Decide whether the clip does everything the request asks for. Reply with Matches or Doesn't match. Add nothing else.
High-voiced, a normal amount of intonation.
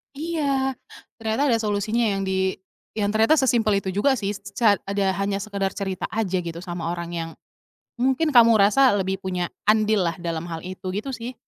Matches